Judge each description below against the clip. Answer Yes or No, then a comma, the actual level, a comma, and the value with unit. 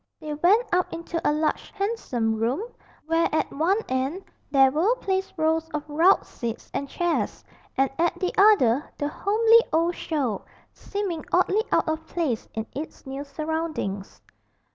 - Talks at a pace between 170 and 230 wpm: No, average, 155 wpm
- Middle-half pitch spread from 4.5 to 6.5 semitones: Yes, average, 4.8 semitones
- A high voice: Yes, very high, 320 Hz